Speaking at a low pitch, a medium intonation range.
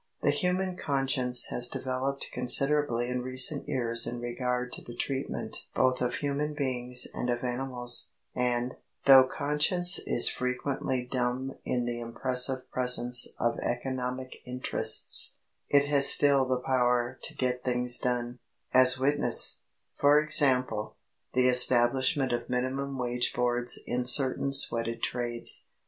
No: low, 125 Hz; narrow, 1.6 semitones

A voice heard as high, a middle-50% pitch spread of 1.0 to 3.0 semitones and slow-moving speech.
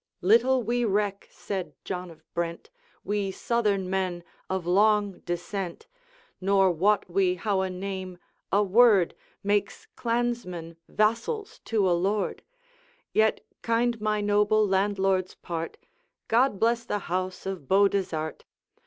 Yes: high, 200 Hz; average, 2.7 semitones; slow, 125 wpm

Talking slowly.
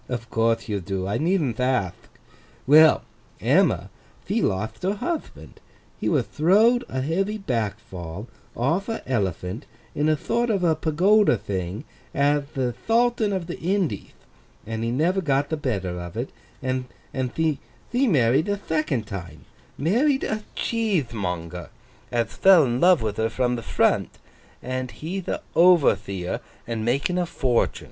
No: average, 145 wpm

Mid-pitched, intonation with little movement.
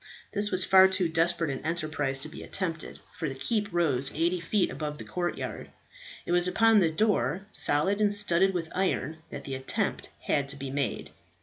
No: medium, 170 Hz; average, 4.2 semitones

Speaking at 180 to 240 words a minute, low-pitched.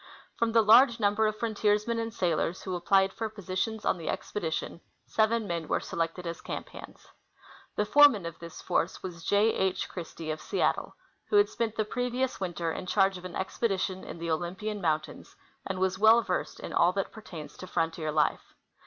No: average, 190 wpm; high, 190 Hz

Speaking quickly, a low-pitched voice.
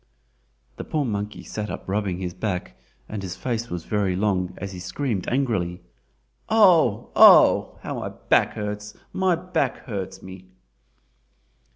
No: average, 140 wpm; low, 105 Hz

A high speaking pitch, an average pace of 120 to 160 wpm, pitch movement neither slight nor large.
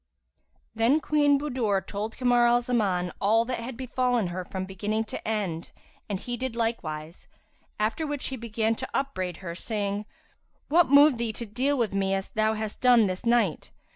No: high, 225 Hz; average, 180 wpm; average, 4.1 semitones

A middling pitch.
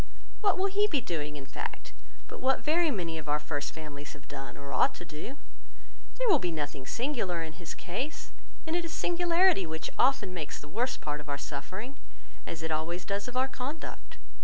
Yes: medium, 180 Hz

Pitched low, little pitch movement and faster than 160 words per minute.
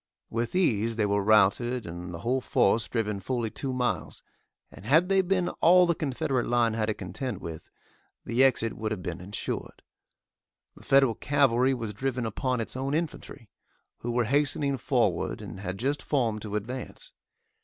No: low, 120 Hz; average, 4.1 semitones; average, 170 wpm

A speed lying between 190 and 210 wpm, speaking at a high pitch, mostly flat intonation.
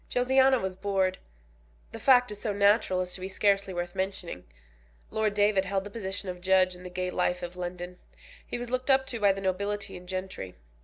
Yes: fast, 205 wpm; high, 195 Hz; narrow, 2.2 semitones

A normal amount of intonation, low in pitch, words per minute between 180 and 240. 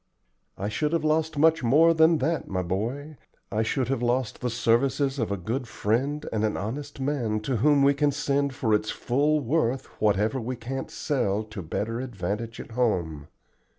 Yes: average, 4.9 semitones; low, 125 Hz; average, 185 wpm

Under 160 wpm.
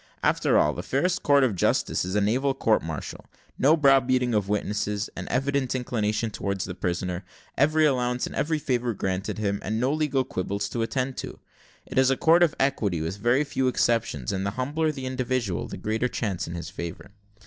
No: average, 200 wpm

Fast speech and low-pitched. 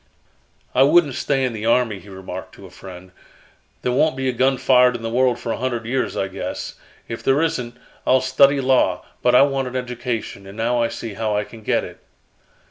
Yes: fast, 215 wpm; low, 125 Hz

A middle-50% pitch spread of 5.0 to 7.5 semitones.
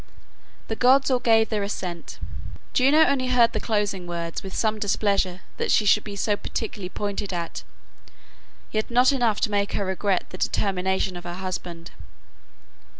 No: average, 3.3 semitones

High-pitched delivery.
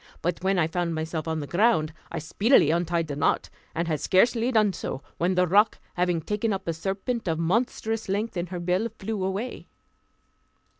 No: medium, 180 Hz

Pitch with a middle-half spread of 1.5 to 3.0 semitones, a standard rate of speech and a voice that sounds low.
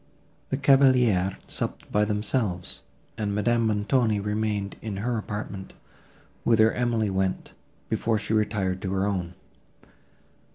No: narrow, 2.5 semitones; slow, 120 wpm; low, 105 Hz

